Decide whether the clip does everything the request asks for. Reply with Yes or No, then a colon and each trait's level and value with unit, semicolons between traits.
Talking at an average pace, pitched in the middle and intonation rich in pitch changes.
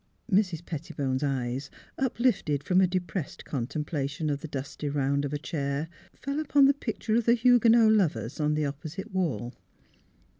Yes: average, 165 wpm; medium, 155 Hz; wide, 7.4 semitones